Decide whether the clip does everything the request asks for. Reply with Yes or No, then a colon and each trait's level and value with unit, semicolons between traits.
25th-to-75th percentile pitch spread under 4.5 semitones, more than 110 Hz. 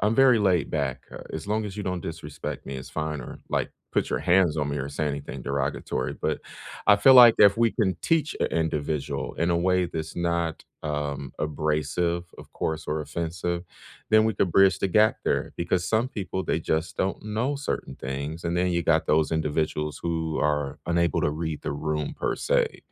No: average, 3.8 semitones; very low, 85 Hz